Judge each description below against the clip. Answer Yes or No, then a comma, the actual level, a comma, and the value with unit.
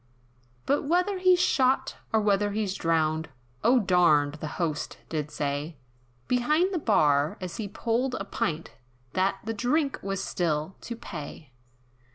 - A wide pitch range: Yes, wide, 8.0 semitones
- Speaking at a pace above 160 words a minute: No, average, 145 wpm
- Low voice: No, high, 195 Hz